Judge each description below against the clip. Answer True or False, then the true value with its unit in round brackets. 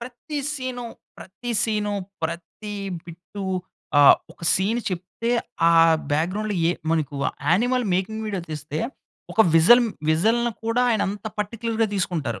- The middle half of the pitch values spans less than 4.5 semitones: False (5.5 semitones)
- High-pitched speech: True (205 Hz)